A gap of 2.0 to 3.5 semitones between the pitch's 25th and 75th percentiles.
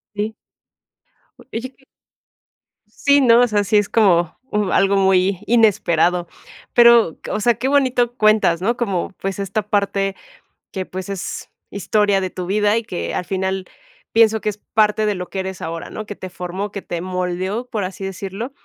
Yes: average, 2.9 semitones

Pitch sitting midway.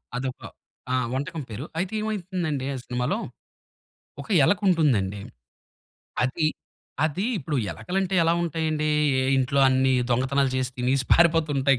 Yes: medium, 145 Hz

